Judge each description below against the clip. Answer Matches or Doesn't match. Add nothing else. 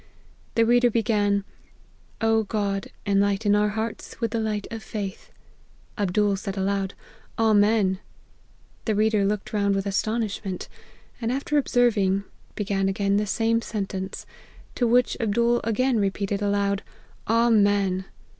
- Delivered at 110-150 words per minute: Matches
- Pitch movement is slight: Matches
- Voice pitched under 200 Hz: Doesn't match